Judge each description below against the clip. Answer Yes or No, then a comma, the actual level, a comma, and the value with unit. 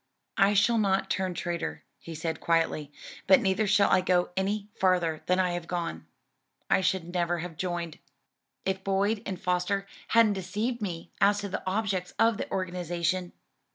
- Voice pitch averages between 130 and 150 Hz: No, medium, 185 Hz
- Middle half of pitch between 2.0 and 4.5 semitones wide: Yes, narrow, 2.4 semitones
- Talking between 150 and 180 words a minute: Yes, average, 165 wpm